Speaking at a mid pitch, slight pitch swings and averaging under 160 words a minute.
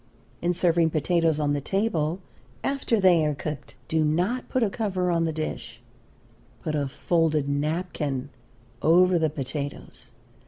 No: medium, 160 Hz; average, 3.2 semitones; average, 145 wpm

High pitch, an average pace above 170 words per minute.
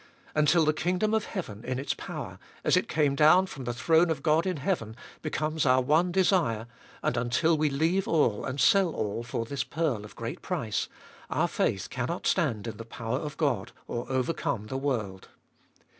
No: medium, 140 Hz; average, 190 wpm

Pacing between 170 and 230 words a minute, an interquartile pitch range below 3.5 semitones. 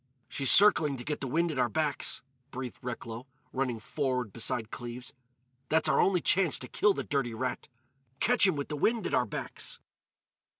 No: average, 175 wpm; average, 4.2 semitones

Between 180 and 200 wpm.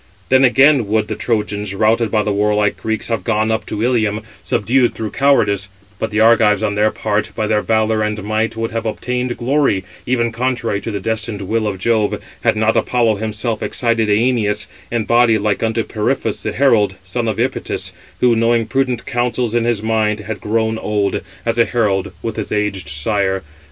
Yes: average, 185 wpm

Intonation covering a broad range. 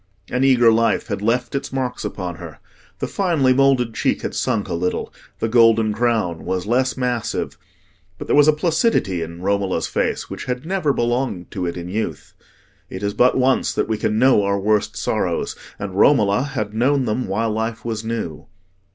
No: average, 4.2 semitones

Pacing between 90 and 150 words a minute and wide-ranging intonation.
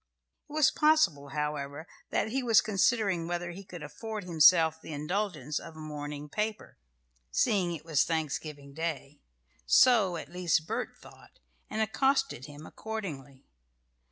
Yes: average, 140 wpm; wide, 6.2 semitones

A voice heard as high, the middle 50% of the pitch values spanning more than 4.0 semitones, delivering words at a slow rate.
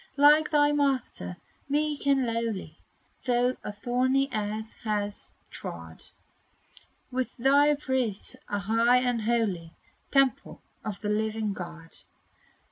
Yes: high, 235 Hz; average, 4.6 semitones; slow, 115 wpm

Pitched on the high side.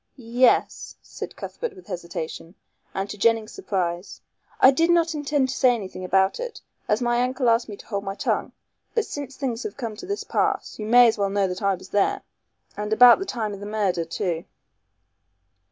Yes: high, 225 Hz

